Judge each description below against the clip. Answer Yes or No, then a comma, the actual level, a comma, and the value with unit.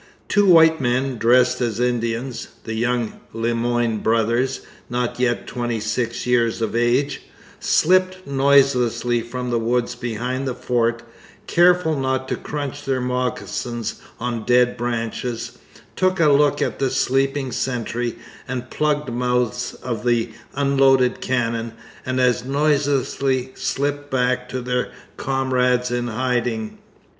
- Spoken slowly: Yes, slow, 130 wpm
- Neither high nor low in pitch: No, low, 125 Hz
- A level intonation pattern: Yes, narrow, 2.2 semitones